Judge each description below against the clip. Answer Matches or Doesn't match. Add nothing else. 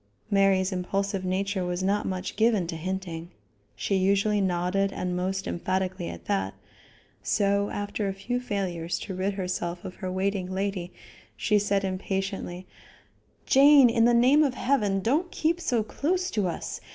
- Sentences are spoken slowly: Doesn't match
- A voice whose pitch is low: Doesn't match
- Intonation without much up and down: Matches